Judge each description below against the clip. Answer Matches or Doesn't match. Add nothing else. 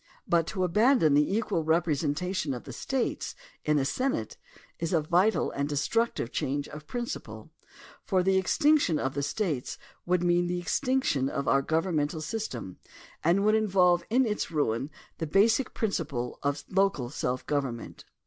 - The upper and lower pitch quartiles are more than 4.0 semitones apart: Matches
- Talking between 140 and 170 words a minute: Matches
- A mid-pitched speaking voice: Matches